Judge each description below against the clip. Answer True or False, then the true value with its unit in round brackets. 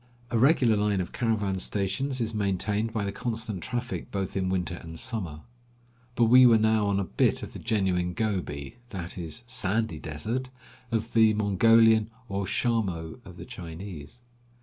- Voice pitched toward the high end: False (105 Hz)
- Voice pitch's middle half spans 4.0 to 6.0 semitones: False (3.6 semitones)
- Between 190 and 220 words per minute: False (170 wpm)